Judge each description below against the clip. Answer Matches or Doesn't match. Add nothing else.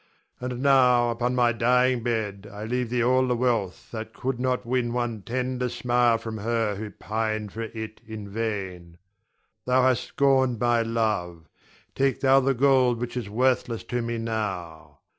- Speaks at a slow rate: Doesn't match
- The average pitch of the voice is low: Matches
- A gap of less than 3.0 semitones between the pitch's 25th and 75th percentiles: Matches